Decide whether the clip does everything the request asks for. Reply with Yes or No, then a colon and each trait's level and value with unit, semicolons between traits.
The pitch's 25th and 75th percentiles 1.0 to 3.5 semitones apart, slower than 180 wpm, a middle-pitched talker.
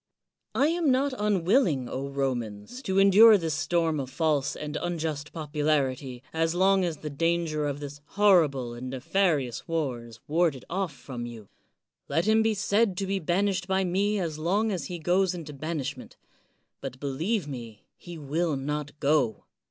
No: wide, 5.5 semitones; average, 165 wpm; medium, 160 Hz